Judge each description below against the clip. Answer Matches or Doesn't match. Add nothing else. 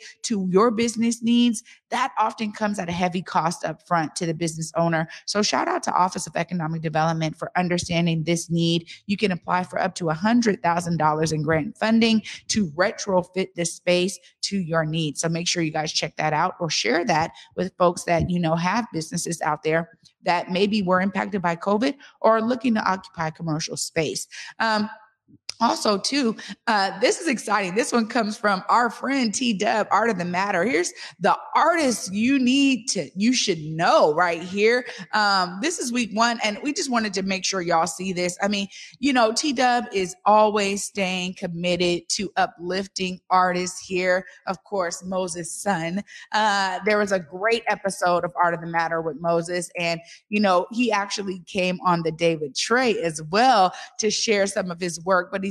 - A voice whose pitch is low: Doesn't match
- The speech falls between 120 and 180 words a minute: Doesn't match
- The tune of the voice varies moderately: Matches